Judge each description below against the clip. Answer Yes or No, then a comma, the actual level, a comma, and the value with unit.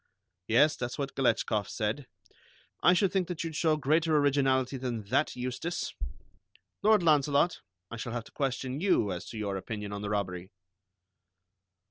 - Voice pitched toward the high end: No, low, 130 Hz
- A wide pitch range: Yes, wide, 6.1 semitones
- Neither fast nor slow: Yes, average, 155 wpm